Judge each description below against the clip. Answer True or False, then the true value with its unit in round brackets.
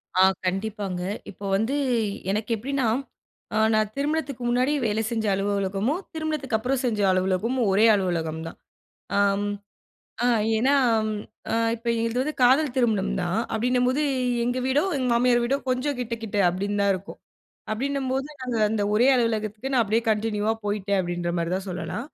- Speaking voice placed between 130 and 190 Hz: False (225 Hz)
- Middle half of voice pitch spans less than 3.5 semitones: False (4.1 semitones)